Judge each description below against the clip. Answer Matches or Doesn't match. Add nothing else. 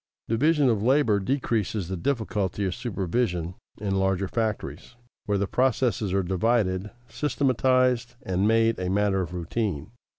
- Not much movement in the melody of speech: Doesn't match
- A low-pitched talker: Matches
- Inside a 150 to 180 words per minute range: Doesn't match